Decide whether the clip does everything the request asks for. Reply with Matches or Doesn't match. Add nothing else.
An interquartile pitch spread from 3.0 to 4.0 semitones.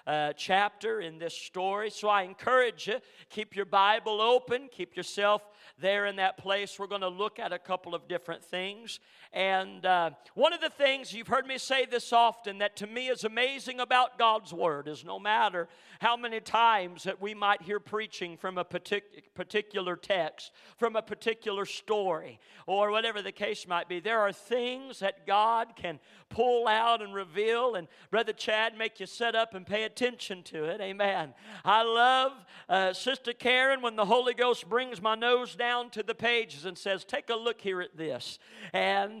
Matches